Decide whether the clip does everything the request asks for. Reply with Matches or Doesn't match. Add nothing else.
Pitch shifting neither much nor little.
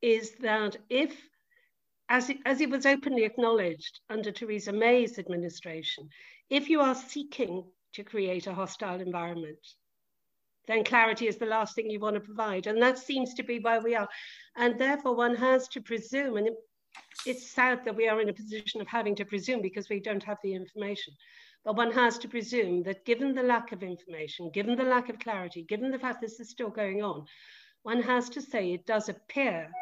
Matches